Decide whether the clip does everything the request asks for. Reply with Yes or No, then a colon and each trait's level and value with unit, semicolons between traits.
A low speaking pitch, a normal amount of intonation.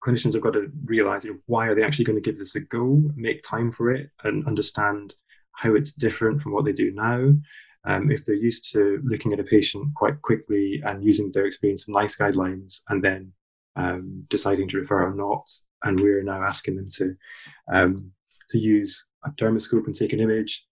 Yes: low, 105 Hz; average, 3.4 semitones